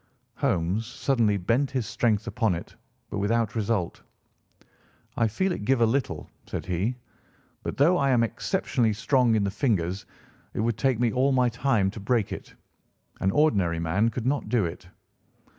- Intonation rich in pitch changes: No, average, 4.1 semitones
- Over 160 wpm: Yes, average, 170 wpm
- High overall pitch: No, low, 115 Hz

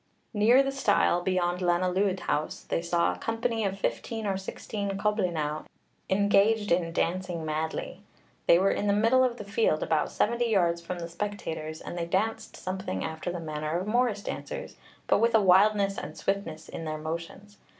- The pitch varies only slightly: No, average, 3.7 semitones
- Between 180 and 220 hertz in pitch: Yes, high, 190 Hz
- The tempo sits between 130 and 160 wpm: No, average, 175 wpm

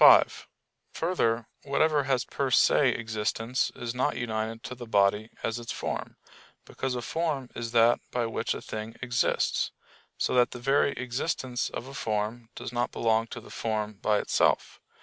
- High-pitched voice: No, low, 120 Hz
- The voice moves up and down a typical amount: No, narrow, 2.3 semitones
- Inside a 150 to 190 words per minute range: Yes, average, 170 wpm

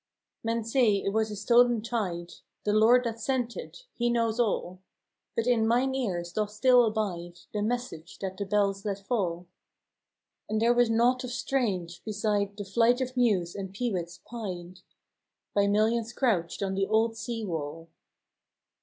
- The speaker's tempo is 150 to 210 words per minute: Yes, average, 170 wpm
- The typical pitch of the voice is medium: No, high, 215 Hz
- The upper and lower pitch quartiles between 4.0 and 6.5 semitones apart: No, average, 3.5 semitones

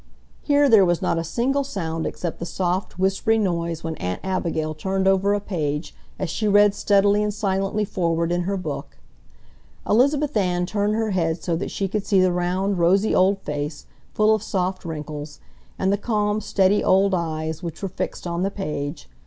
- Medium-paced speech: Yes, average, 185 wpm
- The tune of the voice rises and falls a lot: No, average, 3.5 semitones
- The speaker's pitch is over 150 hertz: Yes, high, 190 Hz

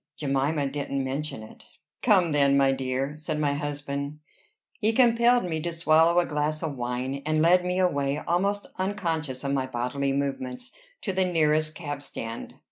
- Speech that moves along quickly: No, average, 165 wpm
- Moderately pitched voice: Yes, medium, 150 Hz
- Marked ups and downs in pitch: No, average, 3.7 semitones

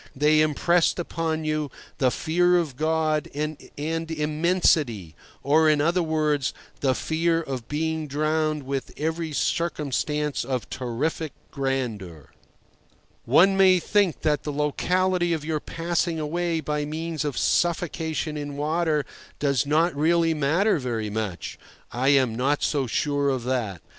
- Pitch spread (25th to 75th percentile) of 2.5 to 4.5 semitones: Yes, average, 2.9 semitones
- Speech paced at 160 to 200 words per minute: No, slow, 135 wpm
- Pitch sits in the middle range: Yes, medium, 155 Hz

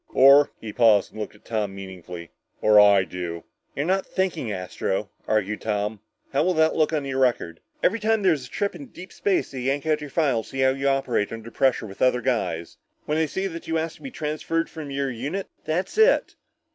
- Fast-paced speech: Yes, fast, 220 wpm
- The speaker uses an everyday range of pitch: No, wide, 7.2 semitones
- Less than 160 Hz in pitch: Yes, low, 135 Hz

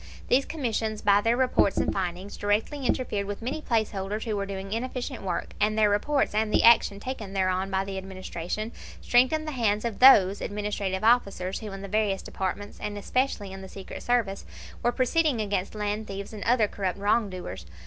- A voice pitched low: No, high, 210 Hz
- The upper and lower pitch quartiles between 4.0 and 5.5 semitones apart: No, average, 3.2 semitones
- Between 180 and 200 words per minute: Yes, average, 190 wpm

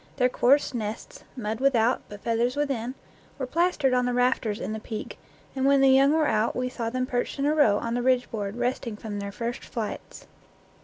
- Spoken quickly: Yes, fast, 215 wpm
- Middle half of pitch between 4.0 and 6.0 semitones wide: No, average, 3.1 semitones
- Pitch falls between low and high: No, high, 245 Hz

